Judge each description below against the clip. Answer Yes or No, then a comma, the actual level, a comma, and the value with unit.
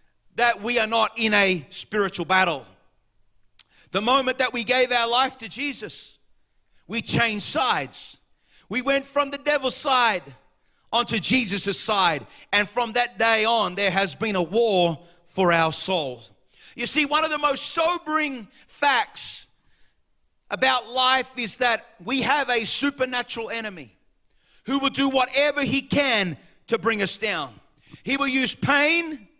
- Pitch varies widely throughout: Yes, wide, 5.8 semitones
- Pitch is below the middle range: No, high, 230 Hz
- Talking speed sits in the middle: Yes, average, 150 wpm